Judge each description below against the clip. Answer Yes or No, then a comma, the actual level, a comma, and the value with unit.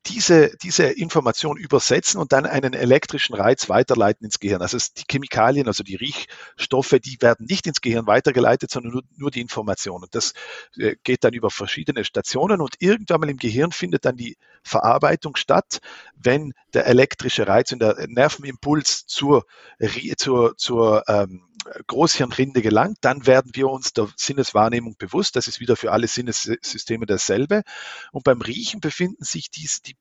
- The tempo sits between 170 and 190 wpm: No, average, 160 wpm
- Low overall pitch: Yes, low, 130 Hz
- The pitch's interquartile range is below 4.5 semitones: No, average, 4.9 semitones